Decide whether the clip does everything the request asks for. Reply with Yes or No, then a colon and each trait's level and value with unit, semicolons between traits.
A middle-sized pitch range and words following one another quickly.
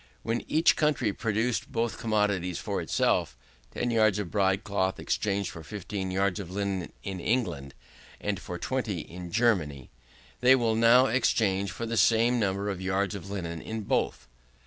No: average, 3.4 semitones; average, 165 wpm